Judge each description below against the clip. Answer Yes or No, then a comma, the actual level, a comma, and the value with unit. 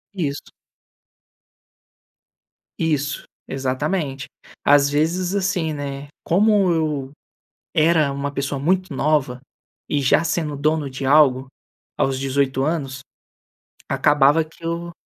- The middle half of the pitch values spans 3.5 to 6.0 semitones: No, average, 3.0 semitones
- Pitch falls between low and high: Yes, medium, 145 Hz